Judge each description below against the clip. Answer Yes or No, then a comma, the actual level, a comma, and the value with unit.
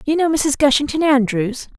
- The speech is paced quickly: No, average, 170 wpm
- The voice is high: Yes, very high, 280 Hz